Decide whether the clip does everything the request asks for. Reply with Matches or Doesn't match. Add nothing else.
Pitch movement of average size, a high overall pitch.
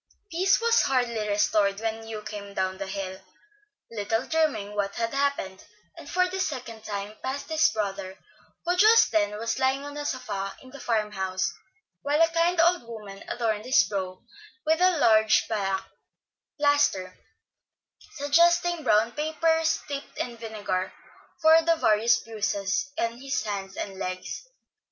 Doesn't match